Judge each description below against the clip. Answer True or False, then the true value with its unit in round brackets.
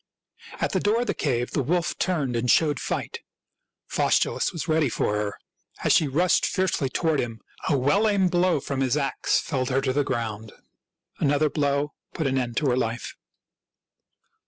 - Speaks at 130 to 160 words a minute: False (180 wpm)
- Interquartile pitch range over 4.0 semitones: True (4.5 semitones)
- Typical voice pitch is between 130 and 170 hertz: True (140 Hz)